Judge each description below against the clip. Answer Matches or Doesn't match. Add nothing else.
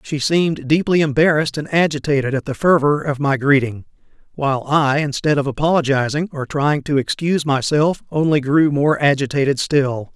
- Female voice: Doesn't match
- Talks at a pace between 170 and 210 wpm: Doesn't match